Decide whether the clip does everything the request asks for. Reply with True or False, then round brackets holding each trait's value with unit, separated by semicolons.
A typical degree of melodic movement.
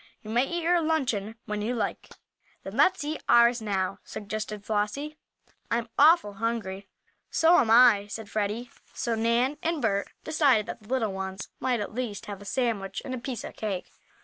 True (4.0 semitones)